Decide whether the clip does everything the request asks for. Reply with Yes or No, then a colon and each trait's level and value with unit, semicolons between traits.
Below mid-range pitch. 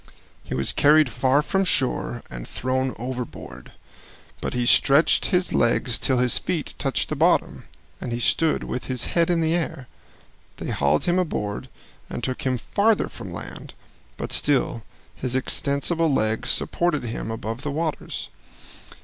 Yes: low, 130 Hz